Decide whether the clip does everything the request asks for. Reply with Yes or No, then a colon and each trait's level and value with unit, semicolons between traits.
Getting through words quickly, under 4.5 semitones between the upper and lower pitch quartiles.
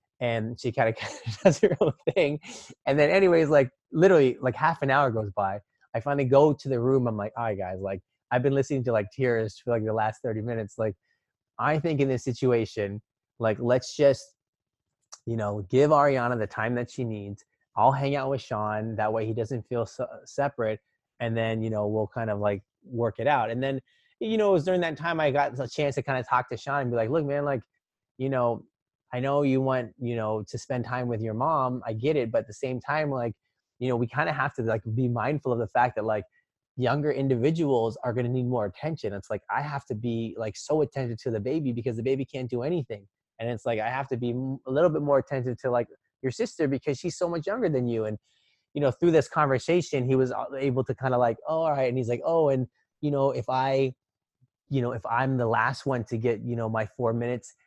Yes: fast, 245 wpm; average, 3.4 semitones